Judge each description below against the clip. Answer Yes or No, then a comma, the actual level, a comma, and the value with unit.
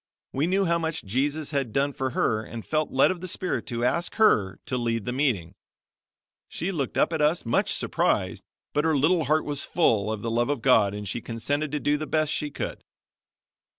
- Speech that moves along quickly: Yes, fast, 215 wpm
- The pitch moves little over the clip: No, average, 5.1 semitones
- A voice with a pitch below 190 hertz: Yes, medium, 140 Hz